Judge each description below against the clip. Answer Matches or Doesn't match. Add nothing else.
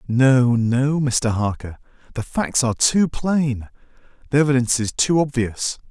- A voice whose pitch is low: Matches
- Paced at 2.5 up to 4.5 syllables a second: Matches